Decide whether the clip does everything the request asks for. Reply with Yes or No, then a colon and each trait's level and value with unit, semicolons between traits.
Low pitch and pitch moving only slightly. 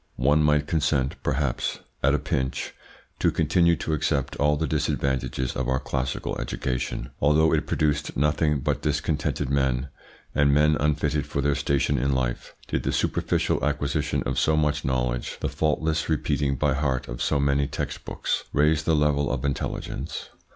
Yes: very low, 70 Hz; narrow, 2.1 semitones